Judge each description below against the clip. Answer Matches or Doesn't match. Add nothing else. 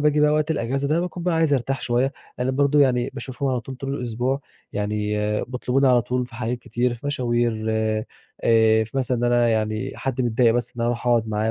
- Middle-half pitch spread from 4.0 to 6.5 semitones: Doesn't match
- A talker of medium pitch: Doesn't match